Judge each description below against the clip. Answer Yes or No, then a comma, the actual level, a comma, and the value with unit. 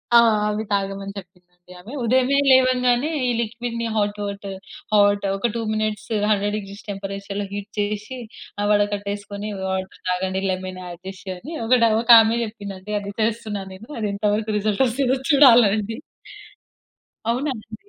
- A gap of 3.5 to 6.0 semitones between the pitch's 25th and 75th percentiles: No, average, 2.7 semitones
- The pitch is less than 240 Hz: Yes, high, 205 Hz